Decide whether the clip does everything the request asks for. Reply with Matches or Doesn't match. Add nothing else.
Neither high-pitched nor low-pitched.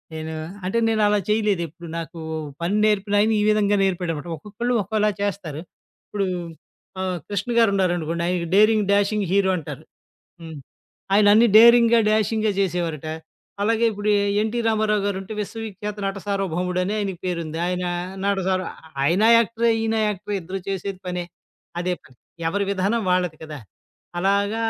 Doesn't match